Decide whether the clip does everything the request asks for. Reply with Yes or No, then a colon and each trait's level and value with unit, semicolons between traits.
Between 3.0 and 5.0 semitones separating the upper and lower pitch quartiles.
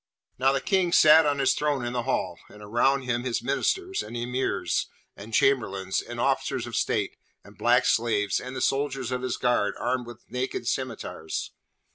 No: narrow, 2.5 semitones